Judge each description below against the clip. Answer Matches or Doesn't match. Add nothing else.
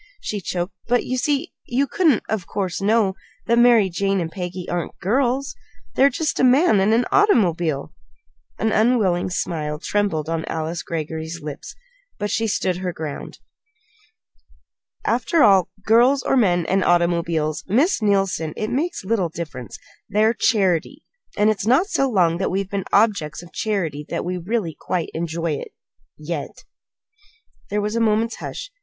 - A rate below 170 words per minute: Matches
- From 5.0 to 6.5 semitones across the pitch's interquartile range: Matches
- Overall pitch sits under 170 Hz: Doesn't match